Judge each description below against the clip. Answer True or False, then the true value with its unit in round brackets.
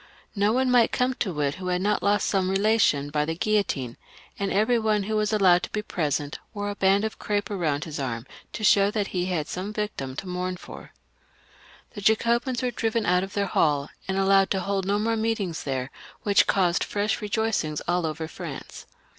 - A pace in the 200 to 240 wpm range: True (205 wpm)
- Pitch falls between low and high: False (195 Hz)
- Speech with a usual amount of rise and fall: True (3.7 semitones)